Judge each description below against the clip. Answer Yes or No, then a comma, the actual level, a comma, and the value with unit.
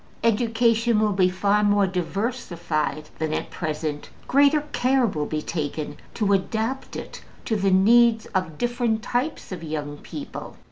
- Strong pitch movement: Yes, wide, 6.4 semitones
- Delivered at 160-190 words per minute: No, average, 145 wpm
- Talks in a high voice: Yes, high, 205 Hz